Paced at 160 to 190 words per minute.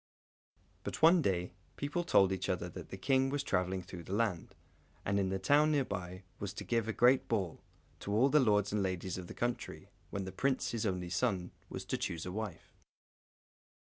No: average, 200 wpm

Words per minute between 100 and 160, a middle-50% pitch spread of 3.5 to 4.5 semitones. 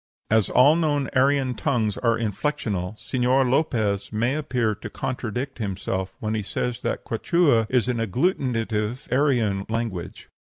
Yes: average, 140 wpm; average, 3.8 semitones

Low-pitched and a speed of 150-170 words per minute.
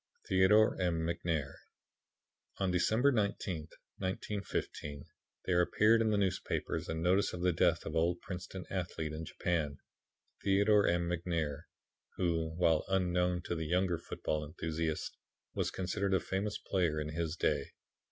No: very low, 90 Hz; average, 140 wpm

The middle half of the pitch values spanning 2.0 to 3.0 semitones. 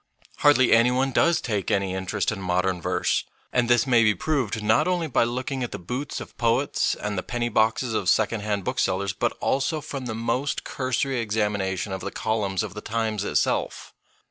No: average, 4.1 semitones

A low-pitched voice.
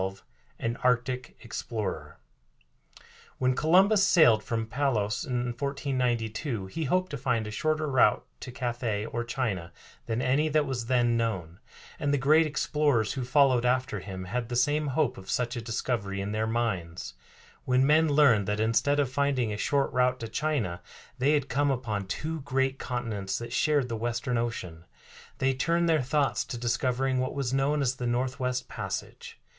Yes: low, 125 Hz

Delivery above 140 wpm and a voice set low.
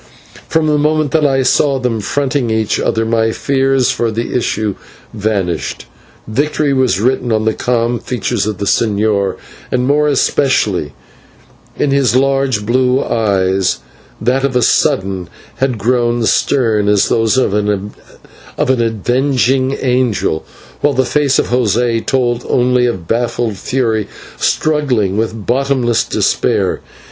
No: slow, 135 wpm; low, 120 Hz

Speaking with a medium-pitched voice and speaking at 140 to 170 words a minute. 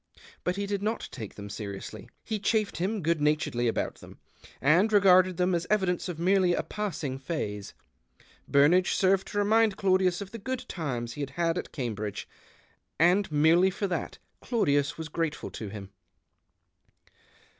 Yes: medium, 175 Hz; average, 160 wpm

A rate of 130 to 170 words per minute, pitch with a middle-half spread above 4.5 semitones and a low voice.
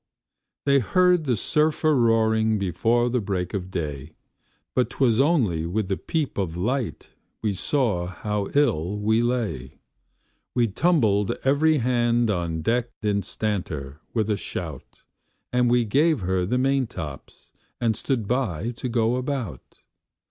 Yes: average, 140 wpm; average, 5.3 semitones; low, 110 Hz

